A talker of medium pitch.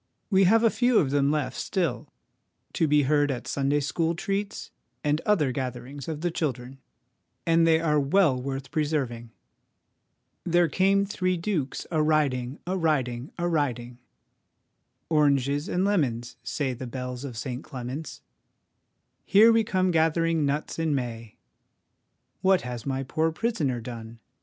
Yes: medium, 150 Hz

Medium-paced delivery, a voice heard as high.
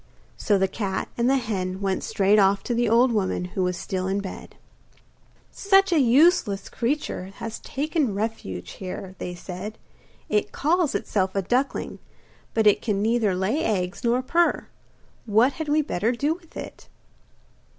Yes: average, 160 wpm; high, 220 Hz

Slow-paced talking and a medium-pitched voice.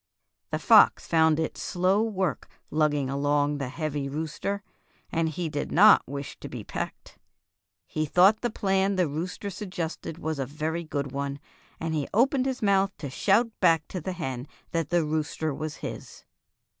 No: average, 170 wpm; medium, 160 Hz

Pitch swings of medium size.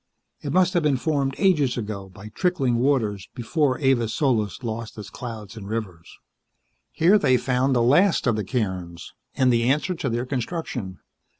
Yes: average, 4.8 semitones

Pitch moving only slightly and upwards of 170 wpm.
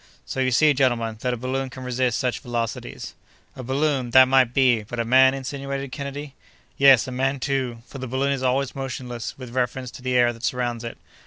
Yes: narrow, 1.8 semitones; average, 195 wpm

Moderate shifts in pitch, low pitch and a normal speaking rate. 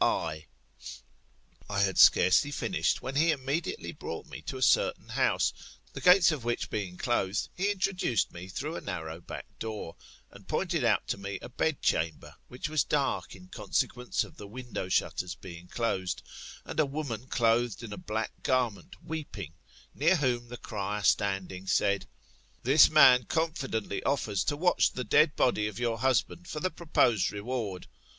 No: wide, 6.6 semitones; low, 120 Hz; average, 165 wpm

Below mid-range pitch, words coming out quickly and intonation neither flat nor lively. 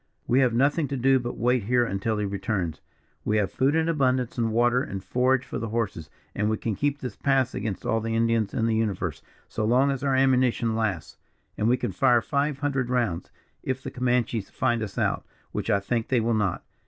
Yes: low, 120 Hz; fast, 220 wpm; average, 3.1 semitones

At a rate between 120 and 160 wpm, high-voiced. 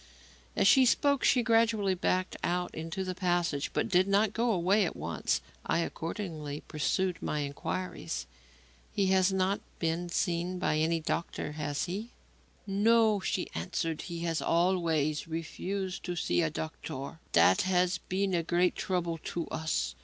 No: average, 155 wpm; medium, 180 Hz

